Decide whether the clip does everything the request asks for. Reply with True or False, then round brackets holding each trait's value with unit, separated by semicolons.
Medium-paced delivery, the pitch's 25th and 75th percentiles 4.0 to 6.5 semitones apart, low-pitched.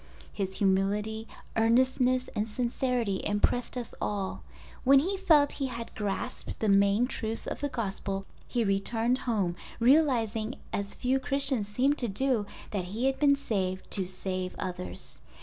False (150 wpm; 4.5 semitones; 225 Hz)